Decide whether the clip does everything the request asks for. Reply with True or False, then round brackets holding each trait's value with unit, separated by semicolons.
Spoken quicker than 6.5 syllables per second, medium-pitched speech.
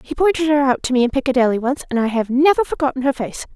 False (6.9 syllables/s; 270 Hz)